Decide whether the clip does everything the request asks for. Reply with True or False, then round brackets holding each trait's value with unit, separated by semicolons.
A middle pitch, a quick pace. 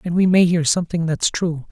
True (170 Hz; 245 wpm)